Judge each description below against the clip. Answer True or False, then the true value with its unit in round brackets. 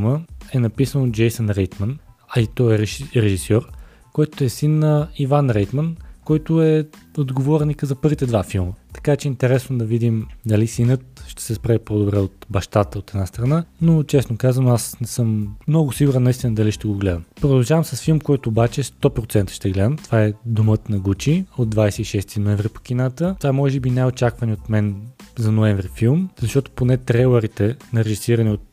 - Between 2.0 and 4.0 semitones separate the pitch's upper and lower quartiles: False (4.6 semitones)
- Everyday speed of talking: False (185 wpm)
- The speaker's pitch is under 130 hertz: True (120 Hz)